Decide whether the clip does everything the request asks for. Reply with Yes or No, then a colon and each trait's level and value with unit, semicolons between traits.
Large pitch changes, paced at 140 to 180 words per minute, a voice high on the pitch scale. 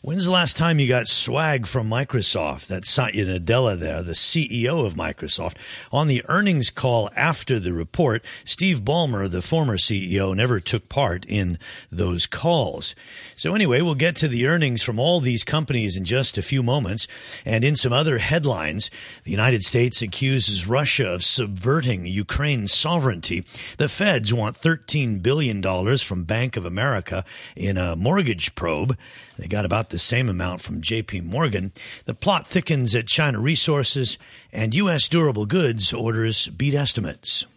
No: wide, 6.2 semitones; average, 160 wpm; low, 120 Hz